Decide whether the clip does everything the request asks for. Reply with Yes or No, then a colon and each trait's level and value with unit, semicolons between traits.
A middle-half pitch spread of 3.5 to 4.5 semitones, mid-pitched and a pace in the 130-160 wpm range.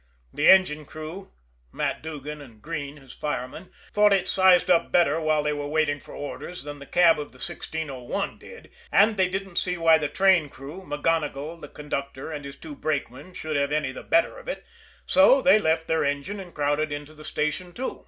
No: average, 3.8 semitones; medium, 155 Hz; average, 200 wpm